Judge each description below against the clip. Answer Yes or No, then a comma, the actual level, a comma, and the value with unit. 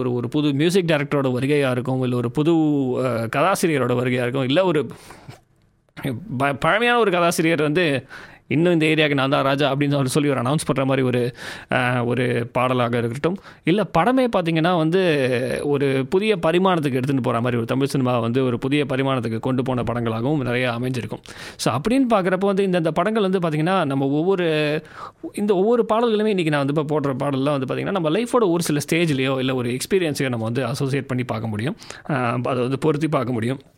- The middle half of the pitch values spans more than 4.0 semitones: Yes, average, 4.7 semitones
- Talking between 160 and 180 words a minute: Yes, average, 175 wpm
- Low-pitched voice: No, medium, 145 Hz